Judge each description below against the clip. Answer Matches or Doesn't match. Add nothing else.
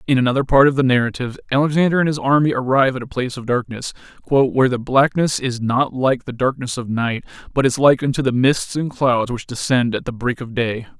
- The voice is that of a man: Matches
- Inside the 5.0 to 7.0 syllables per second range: Matches